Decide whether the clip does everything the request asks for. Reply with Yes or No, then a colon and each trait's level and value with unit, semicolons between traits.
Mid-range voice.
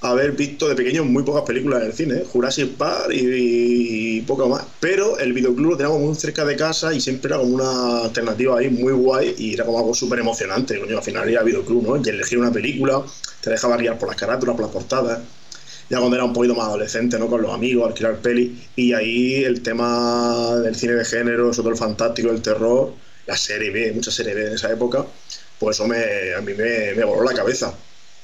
No: low, 120 Hz